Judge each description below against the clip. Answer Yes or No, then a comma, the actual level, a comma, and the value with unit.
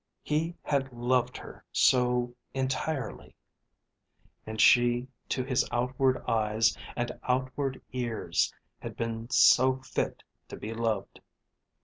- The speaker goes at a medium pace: No, slow, 110 wpm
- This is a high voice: No, low, 125 Hz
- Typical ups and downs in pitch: No, narrow, 2.1 semitones